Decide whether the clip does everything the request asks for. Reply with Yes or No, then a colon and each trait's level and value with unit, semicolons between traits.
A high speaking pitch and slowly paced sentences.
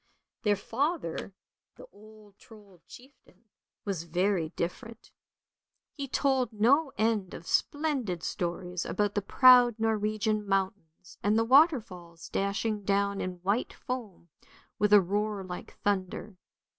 Yes: high, 205 Hz; slow, 120 wpm